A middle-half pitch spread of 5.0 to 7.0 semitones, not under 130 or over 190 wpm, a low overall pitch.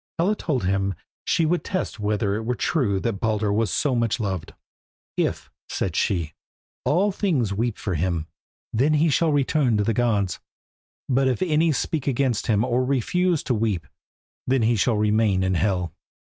Yes: wide, 5.6 semitones; average, 170 wpm; low, 115 Hz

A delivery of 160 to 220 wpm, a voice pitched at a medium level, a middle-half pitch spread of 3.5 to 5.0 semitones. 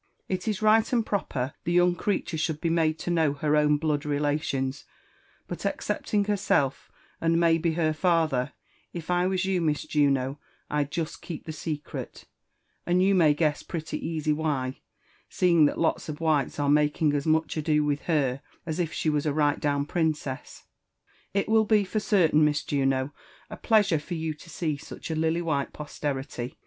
No: average, 180 wpm; medium, 155 Hz; average, 2.9 semitones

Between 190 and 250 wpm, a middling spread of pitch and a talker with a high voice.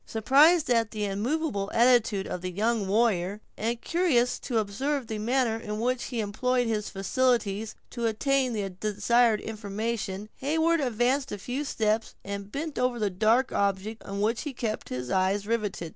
No: average, 170 wpm; average, 3.7 semitones; high, 225 Hz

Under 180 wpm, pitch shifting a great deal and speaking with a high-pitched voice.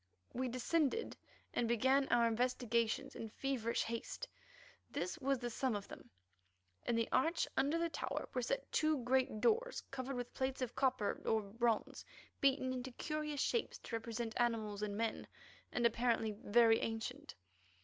No: average, 155 wpm; average, 3.0 semitones; high, 245 Hz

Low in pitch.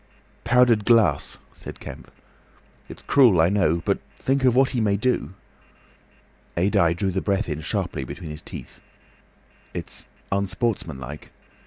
Yes: low, 100 Hz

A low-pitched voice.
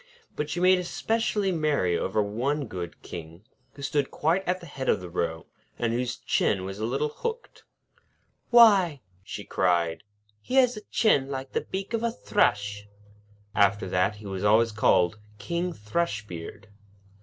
Yes: low, 125 Hz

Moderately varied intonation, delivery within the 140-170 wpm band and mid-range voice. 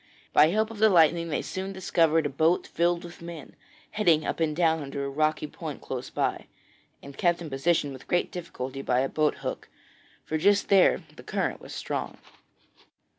No: average, 3.0 semitones; average, 185 wpm; medium, 160 Hz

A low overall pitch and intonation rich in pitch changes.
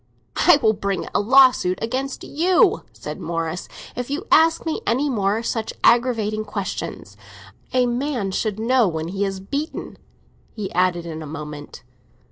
No: high, 220 Hz; wide, 5.7 semitones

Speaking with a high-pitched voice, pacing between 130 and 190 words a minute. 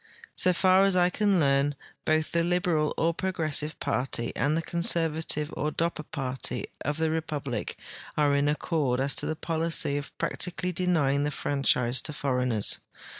No: medium, 155 Hz; average, 160 wpm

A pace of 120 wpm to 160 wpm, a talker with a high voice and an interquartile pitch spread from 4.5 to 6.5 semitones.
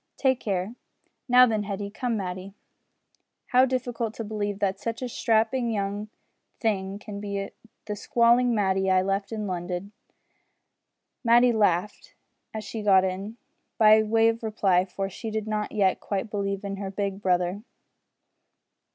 No: average, 150 wpm; high, 205 Hz; narrow, 2.6 semitones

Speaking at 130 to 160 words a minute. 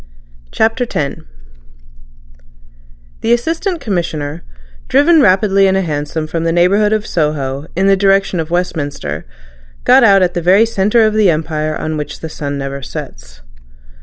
Yes: average, 150 wpm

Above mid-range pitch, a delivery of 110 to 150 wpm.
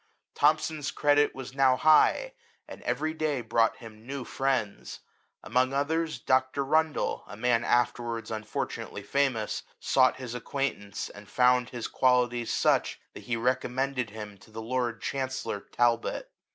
No: low, 125 Hz; average, 140 wpm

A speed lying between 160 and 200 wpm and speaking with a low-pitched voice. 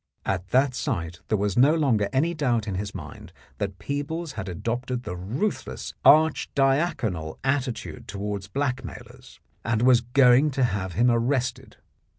No: average, 150 wpm; low, 120 Hz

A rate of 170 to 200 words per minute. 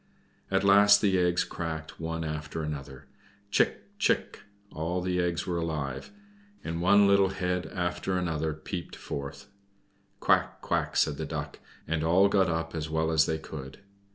No: average, 155 wpm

